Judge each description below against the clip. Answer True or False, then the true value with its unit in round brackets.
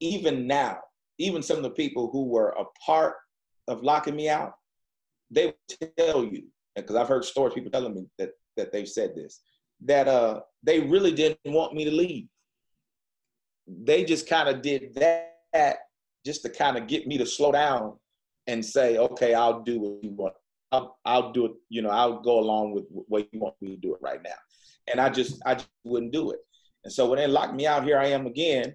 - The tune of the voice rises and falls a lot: True (6.1 semitones)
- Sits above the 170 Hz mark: False (140 Hz)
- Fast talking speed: True (210 wpm)